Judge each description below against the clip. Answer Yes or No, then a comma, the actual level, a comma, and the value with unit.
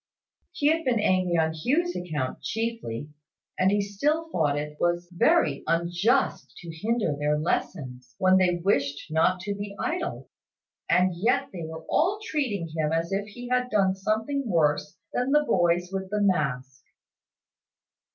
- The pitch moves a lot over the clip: Yes, wide, 6.3 semitones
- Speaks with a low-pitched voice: No, medium, 185 Hz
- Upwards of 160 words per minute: No, average, 155 wpm